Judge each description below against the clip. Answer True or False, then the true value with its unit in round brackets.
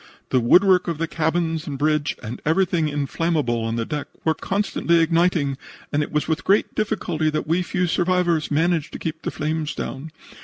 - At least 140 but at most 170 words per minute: False (180 wpm)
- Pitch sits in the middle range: True (160 Hz)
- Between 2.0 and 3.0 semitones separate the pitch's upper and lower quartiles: True (2.7 semitones)